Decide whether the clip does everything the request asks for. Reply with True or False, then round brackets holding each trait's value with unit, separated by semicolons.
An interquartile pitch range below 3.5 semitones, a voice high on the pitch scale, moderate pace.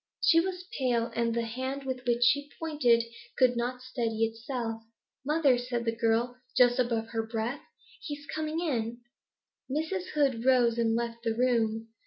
True (2.8 semitones; 245 Hz; 170 wpm)